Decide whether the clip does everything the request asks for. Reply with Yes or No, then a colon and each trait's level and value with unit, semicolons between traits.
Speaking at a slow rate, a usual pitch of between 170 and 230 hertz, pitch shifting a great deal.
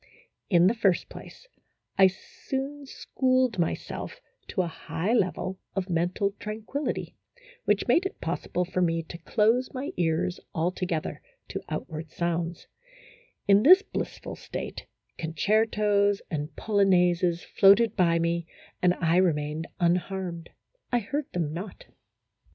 No: slow, 130 wpm; medium, 185 Hz; average, 4.1 semitones